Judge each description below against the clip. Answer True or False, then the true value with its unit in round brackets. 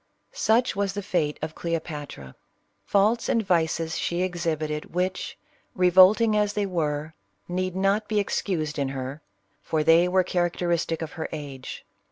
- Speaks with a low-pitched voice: False (175 Hz)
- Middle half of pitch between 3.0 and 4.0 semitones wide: True (3.6 semitones)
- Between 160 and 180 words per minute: False (145 wpm)